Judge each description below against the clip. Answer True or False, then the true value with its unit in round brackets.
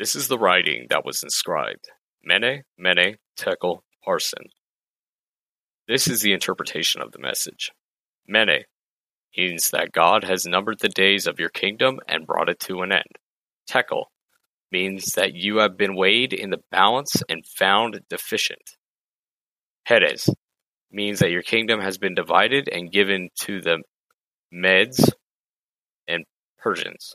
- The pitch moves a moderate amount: False (2.2 semitones)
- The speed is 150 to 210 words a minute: False (140 wpm)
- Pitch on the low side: True (95 Hz)